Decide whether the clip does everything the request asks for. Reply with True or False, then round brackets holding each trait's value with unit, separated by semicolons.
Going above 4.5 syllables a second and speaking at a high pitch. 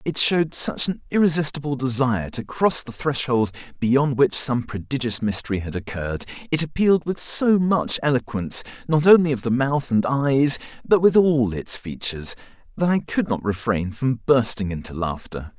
False (5.0 syllables/s; 130 Hz)